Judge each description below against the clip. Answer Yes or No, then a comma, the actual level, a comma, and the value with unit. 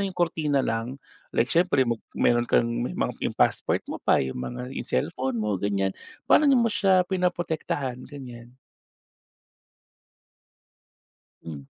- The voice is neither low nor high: No, low, 130 Hz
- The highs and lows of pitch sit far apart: Yes, wide, 7.0 semitones